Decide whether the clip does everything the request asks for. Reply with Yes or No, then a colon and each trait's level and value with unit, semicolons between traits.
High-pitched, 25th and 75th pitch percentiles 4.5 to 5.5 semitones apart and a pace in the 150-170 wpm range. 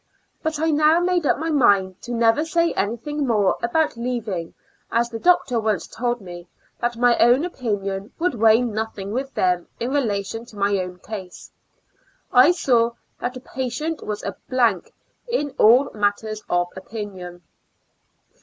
Yes: high, 235 Hz; average, 5.0 semitones; average, 160 wpm